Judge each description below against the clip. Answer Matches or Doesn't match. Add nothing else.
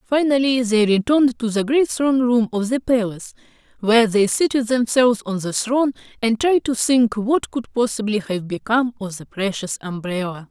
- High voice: Matches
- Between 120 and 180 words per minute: Matches